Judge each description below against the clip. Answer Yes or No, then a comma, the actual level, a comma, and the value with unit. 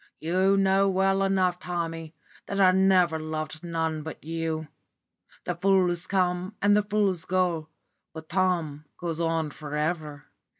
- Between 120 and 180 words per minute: Yes, average, 140 wpm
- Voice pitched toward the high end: No, medium, 175 Hz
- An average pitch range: Yes, average, 3.1 semitones